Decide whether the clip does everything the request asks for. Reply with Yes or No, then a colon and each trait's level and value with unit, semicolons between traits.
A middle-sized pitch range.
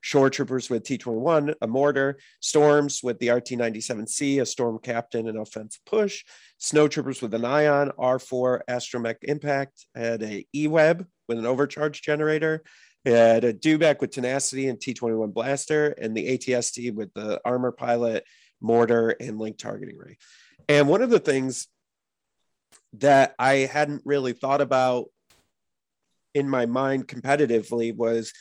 Yes: average, 3.5 semitones